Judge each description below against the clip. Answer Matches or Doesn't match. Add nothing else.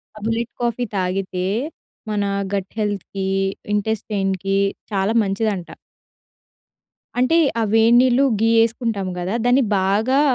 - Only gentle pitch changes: Doesn't match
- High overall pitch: Matches